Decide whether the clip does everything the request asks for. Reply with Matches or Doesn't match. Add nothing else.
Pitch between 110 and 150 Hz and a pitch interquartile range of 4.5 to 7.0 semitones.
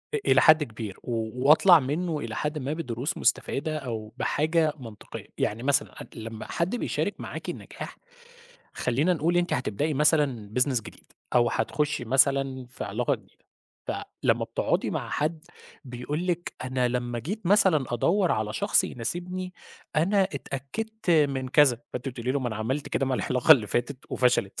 Matches